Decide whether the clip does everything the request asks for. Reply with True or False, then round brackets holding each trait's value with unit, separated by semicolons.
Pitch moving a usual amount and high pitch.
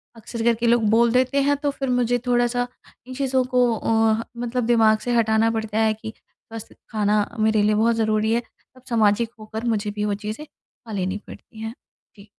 False (1.9 semitones; 225 Hz)